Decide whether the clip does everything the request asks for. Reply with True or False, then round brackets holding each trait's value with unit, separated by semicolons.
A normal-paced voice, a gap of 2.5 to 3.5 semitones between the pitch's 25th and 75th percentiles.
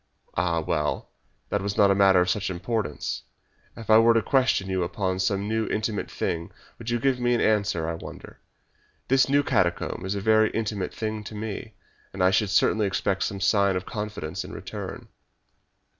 True (185 wpm; 3.1 semitones)